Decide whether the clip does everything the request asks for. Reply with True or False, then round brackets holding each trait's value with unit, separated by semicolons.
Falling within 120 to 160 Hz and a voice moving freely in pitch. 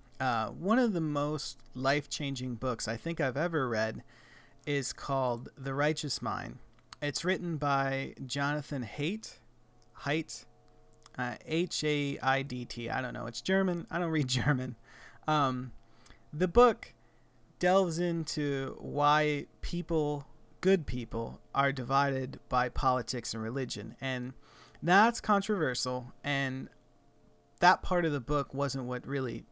False (135 Hz; 3.7 semitones)